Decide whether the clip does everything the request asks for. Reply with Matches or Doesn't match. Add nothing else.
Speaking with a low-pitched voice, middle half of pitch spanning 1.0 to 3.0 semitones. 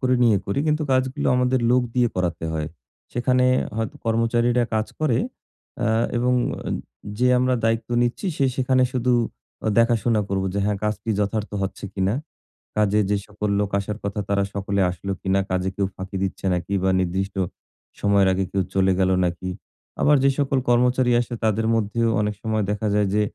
Doesn't match